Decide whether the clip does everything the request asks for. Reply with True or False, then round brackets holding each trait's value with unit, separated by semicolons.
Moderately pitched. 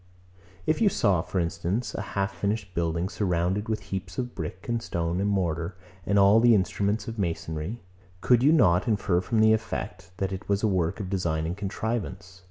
False (95 Hz)